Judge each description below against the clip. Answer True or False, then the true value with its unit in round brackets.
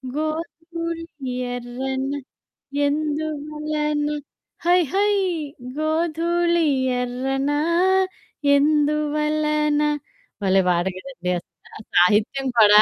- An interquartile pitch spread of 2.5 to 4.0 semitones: True (2.8 semitones)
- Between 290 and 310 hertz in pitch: True (300 Hz)